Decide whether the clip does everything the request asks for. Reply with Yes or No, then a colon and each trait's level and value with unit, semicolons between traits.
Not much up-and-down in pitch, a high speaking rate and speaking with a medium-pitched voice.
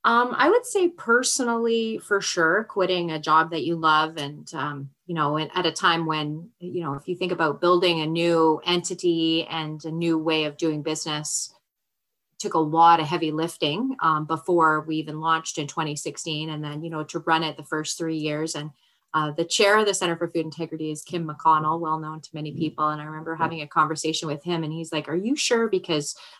Yes: narrow, 2.2 semitones; fast, 215 wpm; medium, 160 Hz